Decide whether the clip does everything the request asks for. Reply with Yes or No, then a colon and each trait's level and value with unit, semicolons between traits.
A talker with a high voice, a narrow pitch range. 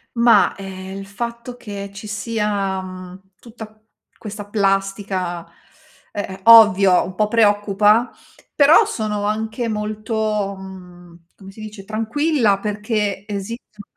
Yes: high, 205 Hz; narrow, 2.1 semitones